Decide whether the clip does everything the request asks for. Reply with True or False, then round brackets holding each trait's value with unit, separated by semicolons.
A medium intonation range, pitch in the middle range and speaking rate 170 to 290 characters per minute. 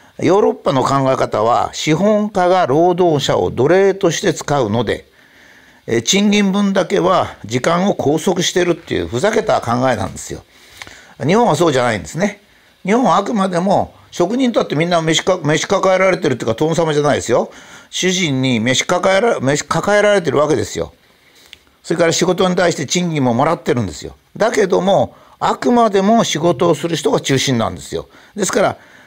False (4.3 semitones; 175 Hz; 360 characters per minute)